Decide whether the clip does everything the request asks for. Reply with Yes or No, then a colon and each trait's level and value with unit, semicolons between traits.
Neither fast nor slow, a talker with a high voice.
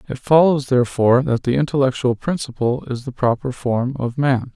No: average, 170 wpm; low, 130 Hz